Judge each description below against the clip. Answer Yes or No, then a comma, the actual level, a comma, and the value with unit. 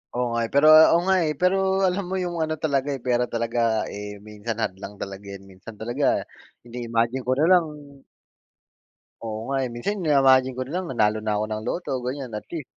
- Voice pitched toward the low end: Yes, low, 125 Hz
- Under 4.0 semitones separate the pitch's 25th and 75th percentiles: No, average, 5.3 semitones